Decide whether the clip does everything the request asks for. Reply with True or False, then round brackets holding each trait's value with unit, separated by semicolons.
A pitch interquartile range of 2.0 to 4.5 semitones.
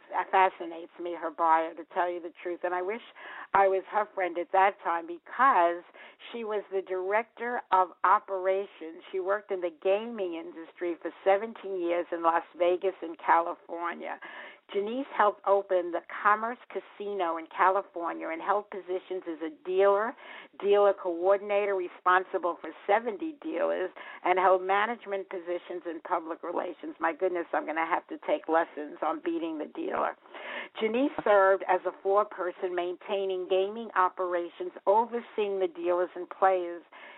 True (2.4 semitones)